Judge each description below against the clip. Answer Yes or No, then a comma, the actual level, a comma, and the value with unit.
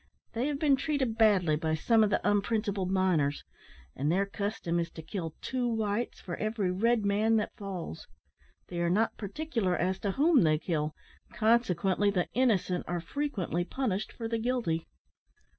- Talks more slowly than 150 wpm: No, average, 165 wpm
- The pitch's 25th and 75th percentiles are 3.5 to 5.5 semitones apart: Yes, average, 4.6 semitones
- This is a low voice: No, high, 200 Hz